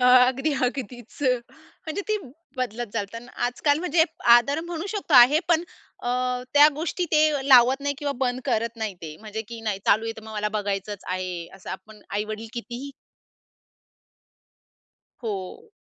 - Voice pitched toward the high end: Yes, high, 240 Hz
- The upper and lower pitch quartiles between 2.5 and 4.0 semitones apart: No, average, 5.0 semitones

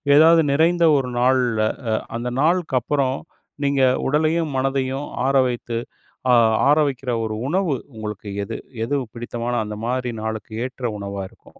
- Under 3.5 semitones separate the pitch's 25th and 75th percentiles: No, average, 3.8 semitones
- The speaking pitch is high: No, low, 130 Hz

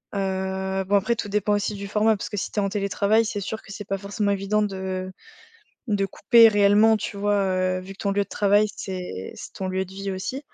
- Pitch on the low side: No, high, 200 Hz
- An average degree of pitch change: No, narrow, 1.5 semitones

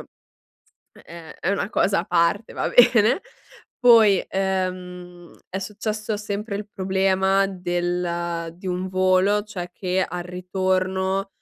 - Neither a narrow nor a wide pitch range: No, narrow, 1.9 semitones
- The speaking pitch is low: No, high, 190 Hz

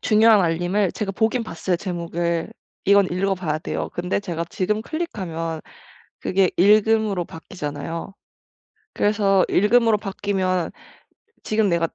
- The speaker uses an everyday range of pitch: Yes, average, 3.6 semitones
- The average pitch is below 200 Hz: Yes, high, 190 Hz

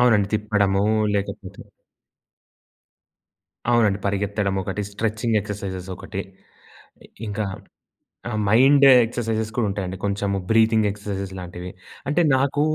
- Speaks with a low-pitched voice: Yes, low, 105 Hz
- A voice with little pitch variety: Yes, narrow, 2.2 semitones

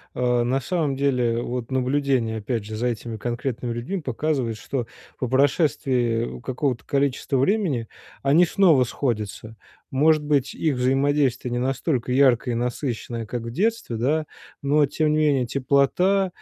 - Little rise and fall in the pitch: No, average, 3.3 semitones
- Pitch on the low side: Yes, low, 130 Hz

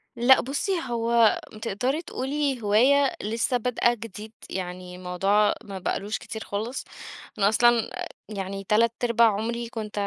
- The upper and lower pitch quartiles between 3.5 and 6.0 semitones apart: No, average, 2.9 semitones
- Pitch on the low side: No, high, 225 Hz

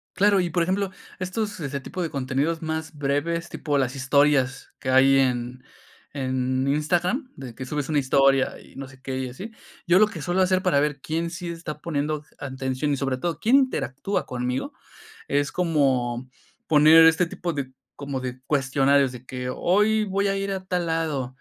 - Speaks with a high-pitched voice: No, medium, 145 Hz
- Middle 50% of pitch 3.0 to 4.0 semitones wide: No, average, 4.7 semitones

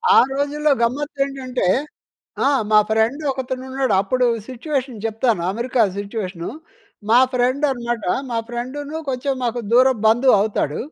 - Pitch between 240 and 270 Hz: Yes, very high, 250 Hz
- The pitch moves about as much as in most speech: Yes, average, 3.1 semitones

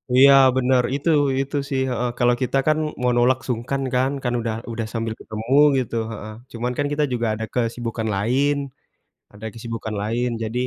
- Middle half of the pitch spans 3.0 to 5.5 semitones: No, narrow, 2.5 semitones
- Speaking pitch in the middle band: No, low, 120 Hz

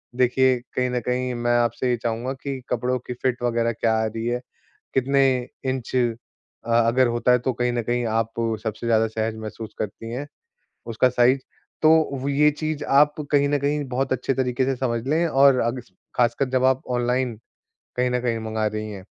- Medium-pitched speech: No, low, 125 Hz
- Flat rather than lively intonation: Yes, narrow, 2.2 semitones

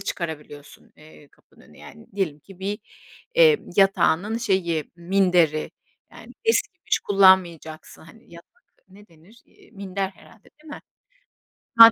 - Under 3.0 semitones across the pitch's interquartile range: No, average, 4.1 semitones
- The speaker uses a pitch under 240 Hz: Yes, high, 190 Hz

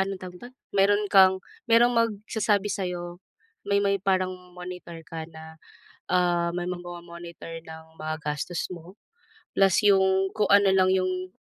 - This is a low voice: No, medium, 185 Hz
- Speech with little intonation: Yes, narrow, 2.2 semitones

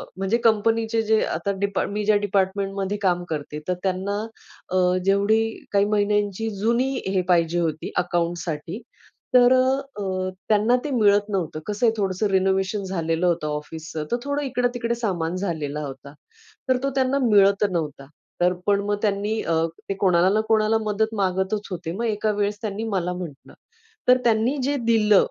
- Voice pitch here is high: Yes, high, 200 Hz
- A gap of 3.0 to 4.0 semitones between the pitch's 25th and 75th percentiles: Yes, average, 3.4 semitones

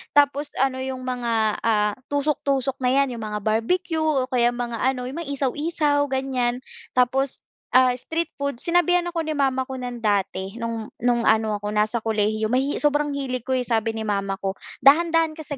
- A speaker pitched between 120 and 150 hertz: No, very high, 255 Hz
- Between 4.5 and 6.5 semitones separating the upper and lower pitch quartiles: No, average, 4.1 semitones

